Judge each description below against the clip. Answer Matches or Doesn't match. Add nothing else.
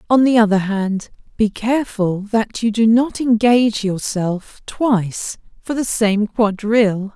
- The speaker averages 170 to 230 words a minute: Doesn't match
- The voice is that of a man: Doesn't match